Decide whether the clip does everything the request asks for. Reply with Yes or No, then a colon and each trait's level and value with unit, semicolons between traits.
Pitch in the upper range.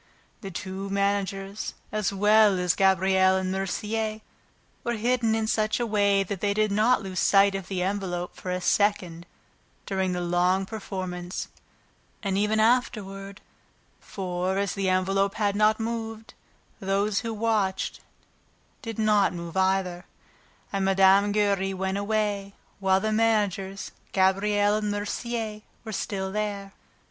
Yes: high, 200 Hz